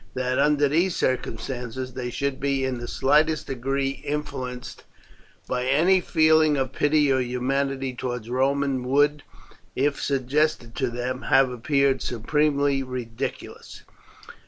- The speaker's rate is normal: No, slow, 125 wpm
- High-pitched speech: No, low, 135 Hz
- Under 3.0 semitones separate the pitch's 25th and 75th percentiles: Yes, narrow, 2.4 semitones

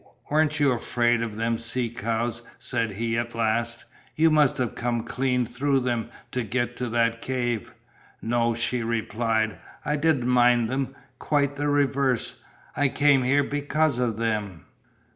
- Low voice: Yes, low, 120 Hz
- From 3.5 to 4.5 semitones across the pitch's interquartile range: No, average, 2.8 semitones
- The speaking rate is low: No, average, 155 wpm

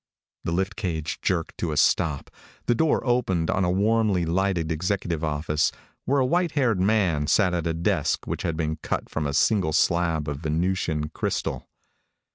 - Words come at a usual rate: Yes, average, 175 wpm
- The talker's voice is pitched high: No, very low, 85 Hz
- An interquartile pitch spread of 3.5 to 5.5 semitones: Yes, average, 4.2 semitones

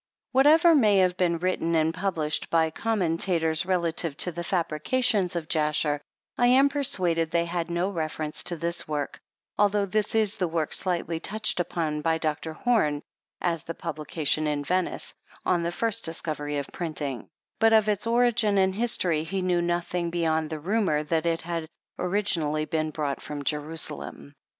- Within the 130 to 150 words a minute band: No, average, 165 wpm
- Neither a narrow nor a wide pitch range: Yes, average, 3.8 semitones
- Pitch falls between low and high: Yes, medium, 170 Hz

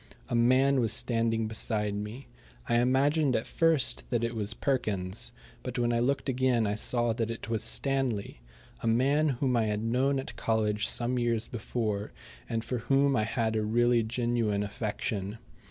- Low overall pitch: Yes, low, 115 Hz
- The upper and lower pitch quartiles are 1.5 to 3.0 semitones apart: Yes, narrow, 2.6 semitones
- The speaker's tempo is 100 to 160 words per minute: No, average, 170 wpm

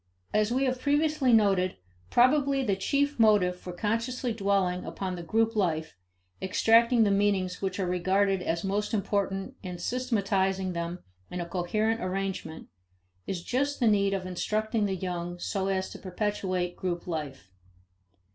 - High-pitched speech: Yes, high, 195 Hz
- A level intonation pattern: No, average, 3.7 semitones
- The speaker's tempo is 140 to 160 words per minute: Yes, average, 150 wpm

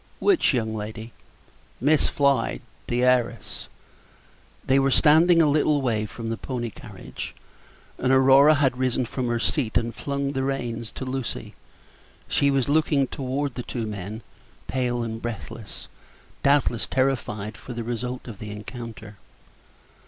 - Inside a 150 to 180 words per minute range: No, average, 140 wpm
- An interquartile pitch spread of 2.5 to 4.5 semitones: Yes, average, 3.2 semitones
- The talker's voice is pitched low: Yes, low, 125 Hz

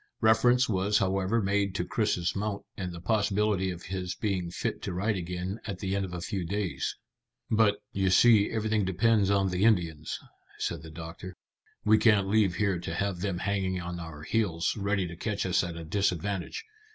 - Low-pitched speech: Yes, very low, 95 Hz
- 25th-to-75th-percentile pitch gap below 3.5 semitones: Yes, average, 2.9 semitones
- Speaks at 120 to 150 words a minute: No, average, 190 wpm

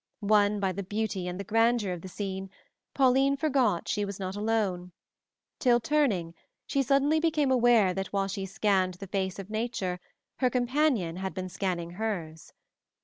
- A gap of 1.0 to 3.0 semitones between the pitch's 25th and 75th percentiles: No, average, 4.6 semitones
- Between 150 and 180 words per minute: Yes, average, 165 wpm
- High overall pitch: Yes, high, 205 Hz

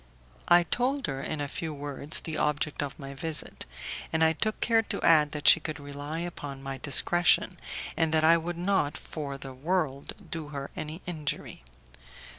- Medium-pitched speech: Yes, medium, 155 Hz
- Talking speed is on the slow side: No, average, 180 wpm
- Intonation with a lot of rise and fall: No, average, 2.8 semitones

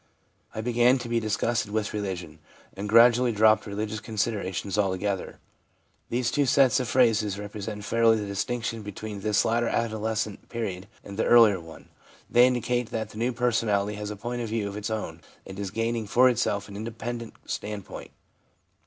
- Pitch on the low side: Yes, low, 110 Hz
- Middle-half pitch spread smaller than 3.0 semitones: Yes, narrow, 2.4 semitones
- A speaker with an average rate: Yes, average, 170 wpm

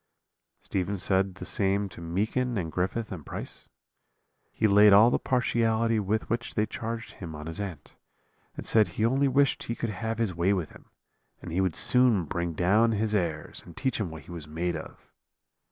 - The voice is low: Yes, low, 100 Hz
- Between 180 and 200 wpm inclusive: Yes, average, 195 wpm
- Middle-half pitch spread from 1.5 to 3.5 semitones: No, average, 4.6 semitones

